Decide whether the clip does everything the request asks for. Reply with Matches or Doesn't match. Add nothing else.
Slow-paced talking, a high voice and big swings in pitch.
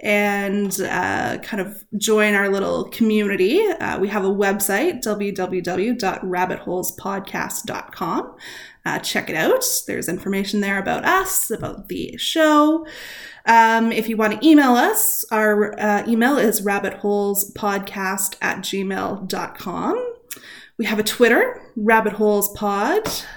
Doesn't match